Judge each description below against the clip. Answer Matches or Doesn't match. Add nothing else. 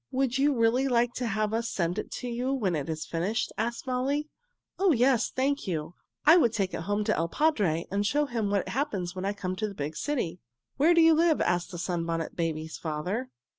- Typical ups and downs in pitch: Doesn't match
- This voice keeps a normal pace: Doesn't match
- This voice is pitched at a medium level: Doesn't match